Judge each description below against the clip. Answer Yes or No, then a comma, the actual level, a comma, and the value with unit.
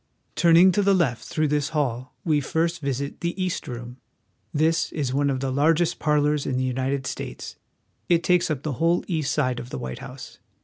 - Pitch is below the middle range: No, medium, 150 Hz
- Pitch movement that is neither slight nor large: Yes, average, 4.2 semitones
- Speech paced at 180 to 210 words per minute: Yes, average, 200 wpm